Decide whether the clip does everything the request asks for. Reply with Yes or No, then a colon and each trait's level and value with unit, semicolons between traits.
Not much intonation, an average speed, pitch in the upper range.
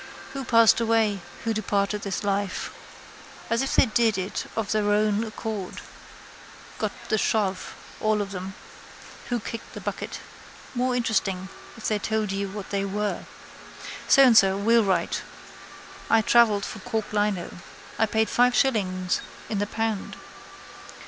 Yes: narrow, 2.3 semitones; average, 145 wpm; high, 210 Hz